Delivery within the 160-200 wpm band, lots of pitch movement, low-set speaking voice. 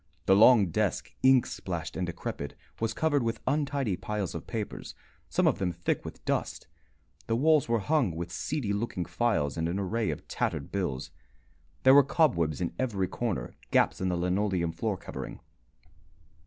Yes: average, 170 wpm; wide, 5.7 semitones; low, 100 Hz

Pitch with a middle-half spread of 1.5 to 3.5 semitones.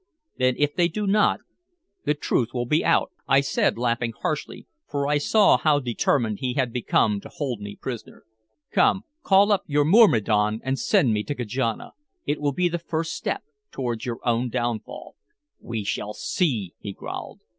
No: average, 4.7 semitones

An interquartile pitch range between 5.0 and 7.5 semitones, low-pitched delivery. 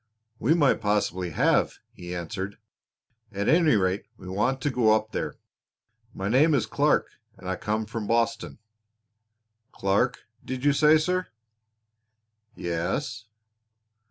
Yes: wide, 5.6 semitones; low, 110 Hz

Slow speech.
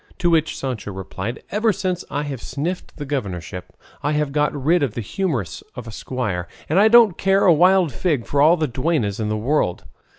No: fast, 205 wpm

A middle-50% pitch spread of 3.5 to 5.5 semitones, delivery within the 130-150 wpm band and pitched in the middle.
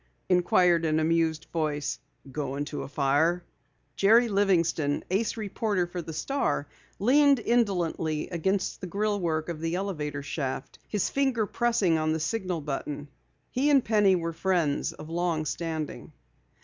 Yes: average, 4.5 semitones; average, 140 wpm; medium, 170 Hz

